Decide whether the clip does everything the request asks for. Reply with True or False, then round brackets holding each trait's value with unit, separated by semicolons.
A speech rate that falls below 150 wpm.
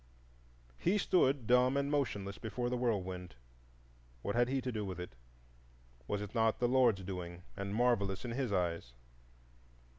False (155 wpm)